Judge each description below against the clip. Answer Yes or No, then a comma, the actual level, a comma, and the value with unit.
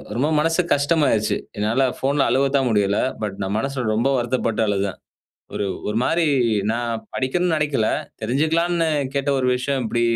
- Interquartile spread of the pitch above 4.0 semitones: Yes, average, 4.5 semitones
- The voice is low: Yes, low, 130 Hz